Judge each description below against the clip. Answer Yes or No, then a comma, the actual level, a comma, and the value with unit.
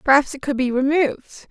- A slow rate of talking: No, average, 200 wpm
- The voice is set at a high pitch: Yes, very high, 275 Hz